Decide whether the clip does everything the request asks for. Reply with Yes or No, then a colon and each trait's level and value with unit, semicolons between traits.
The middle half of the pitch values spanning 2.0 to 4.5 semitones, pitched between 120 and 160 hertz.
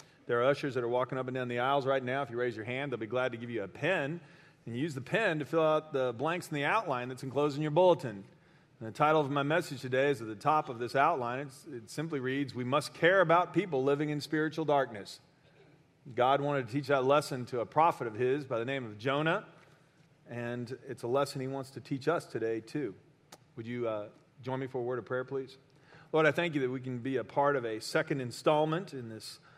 Yes: average, 3.4 semitones; medium, 140 Hz